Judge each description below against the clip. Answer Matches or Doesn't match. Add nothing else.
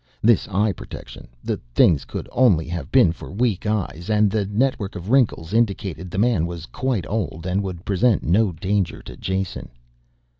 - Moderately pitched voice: Doesn't match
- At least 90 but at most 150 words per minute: Doesn't match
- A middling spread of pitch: Matches